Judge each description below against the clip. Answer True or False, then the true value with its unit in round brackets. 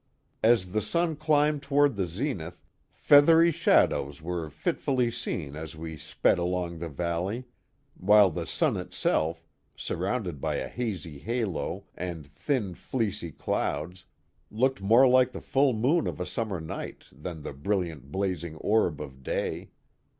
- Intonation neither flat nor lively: False (7.3 semitones)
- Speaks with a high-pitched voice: False (95 Hz)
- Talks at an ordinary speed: True (145 wpm)